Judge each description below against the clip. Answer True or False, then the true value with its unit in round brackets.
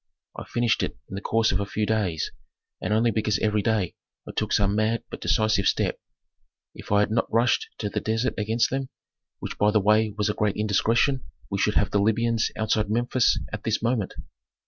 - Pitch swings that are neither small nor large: False (1.7 semitones)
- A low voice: True (110 Hz)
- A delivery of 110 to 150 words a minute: False (205 wpm)